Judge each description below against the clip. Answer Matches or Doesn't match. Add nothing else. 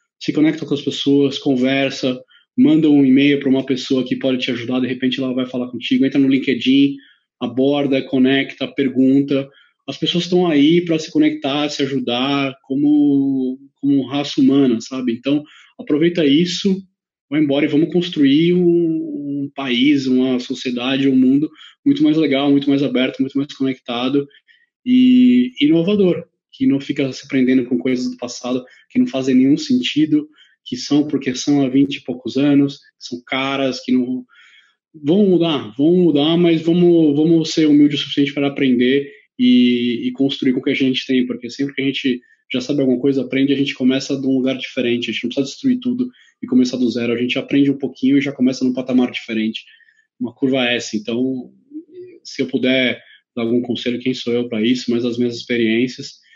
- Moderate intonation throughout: Matches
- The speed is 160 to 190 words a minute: Matches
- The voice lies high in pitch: Doesn't match